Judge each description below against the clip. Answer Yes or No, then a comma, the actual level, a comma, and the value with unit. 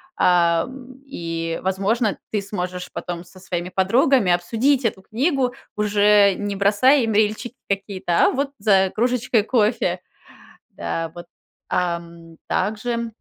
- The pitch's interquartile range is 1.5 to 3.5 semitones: No, average, 4.8 semitones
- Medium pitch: No, high, 205 Hz